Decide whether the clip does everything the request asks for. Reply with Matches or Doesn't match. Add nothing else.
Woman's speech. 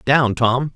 Doesn't match